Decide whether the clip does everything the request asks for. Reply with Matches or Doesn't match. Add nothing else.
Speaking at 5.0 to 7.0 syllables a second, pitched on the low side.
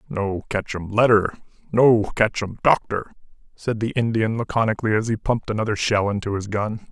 Matches